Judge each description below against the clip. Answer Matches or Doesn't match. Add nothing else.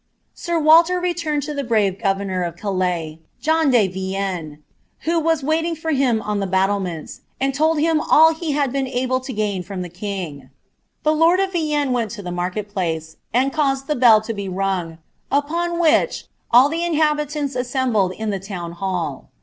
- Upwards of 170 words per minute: Matches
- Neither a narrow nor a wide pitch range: Doesn't match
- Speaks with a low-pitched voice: Doesn't match